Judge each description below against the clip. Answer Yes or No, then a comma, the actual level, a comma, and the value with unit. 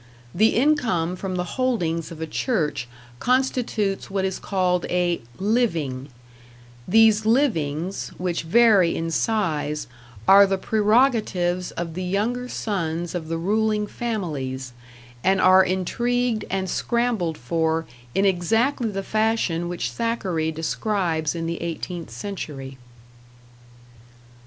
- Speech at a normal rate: No, slow, 120 wpm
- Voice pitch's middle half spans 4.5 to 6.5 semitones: Yes, average, 5.0 semitones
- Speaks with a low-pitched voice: No, medium, 185 Hz